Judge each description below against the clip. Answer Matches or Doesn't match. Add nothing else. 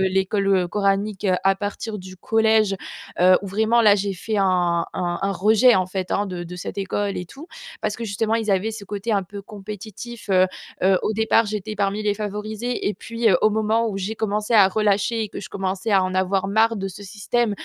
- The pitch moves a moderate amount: Doesn't match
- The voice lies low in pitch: Doesn't match